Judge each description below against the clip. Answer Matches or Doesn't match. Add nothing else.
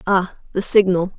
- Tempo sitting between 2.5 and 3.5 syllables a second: Doesn't match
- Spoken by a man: Doesn't match